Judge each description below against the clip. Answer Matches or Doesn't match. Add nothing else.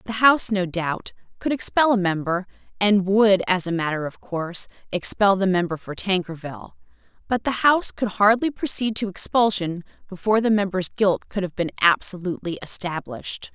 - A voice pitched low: Doesn't match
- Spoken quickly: Doesn't match